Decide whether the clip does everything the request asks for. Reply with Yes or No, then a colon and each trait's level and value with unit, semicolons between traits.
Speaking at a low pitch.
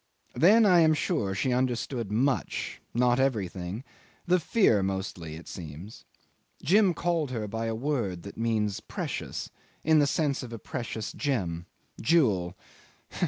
Yes: low, 115 Hz